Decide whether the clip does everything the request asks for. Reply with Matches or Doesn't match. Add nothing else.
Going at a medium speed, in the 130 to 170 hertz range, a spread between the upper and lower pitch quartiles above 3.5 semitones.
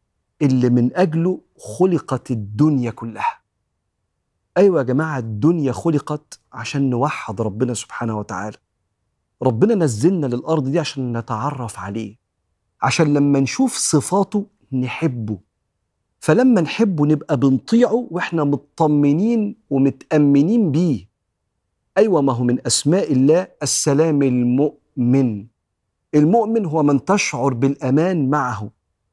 Matches